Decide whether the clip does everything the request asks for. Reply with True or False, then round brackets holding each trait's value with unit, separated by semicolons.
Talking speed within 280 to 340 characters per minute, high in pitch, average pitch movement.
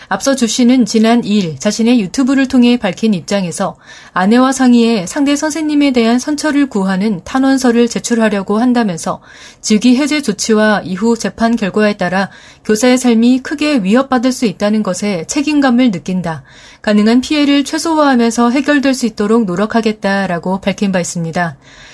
False (355 characters per minute; 230 Hz; 4.4 semitones)